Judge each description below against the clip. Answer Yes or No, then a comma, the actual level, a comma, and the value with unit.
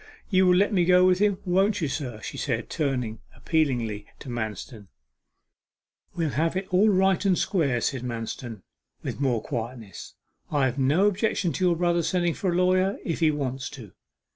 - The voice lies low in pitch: No, medium, 155 Hz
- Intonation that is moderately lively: No, wide, 6.8 semitones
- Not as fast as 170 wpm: No, average, 180 wpm